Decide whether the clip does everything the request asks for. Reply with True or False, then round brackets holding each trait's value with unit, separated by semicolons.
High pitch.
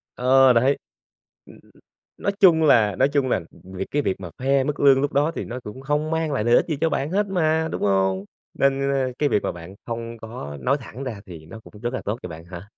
False (130 Hz)